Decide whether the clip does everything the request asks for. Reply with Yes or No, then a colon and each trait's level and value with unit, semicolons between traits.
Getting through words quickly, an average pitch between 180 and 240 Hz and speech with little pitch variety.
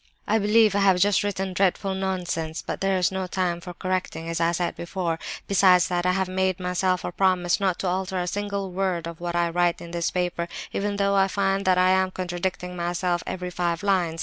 Yes: fast, 215 wpm; medium, 185 Hz; narrow, 1.7 semitones